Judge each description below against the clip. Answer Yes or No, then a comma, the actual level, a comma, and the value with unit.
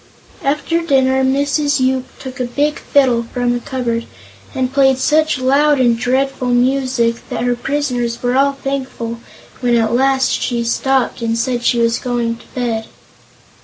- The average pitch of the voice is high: Yes, very high, 255 Hz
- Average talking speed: Yes, average, 165 wpm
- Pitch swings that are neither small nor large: No, narrow, 2.3 semitones